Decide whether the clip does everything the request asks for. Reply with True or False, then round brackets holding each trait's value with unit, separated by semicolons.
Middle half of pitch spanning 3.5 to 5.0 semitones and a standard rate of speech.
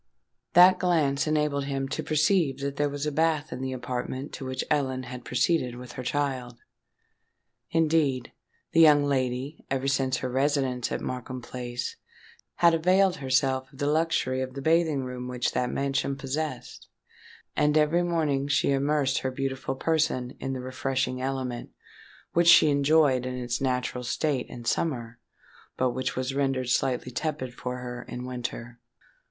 False (2.8 semitones; 160 wpm)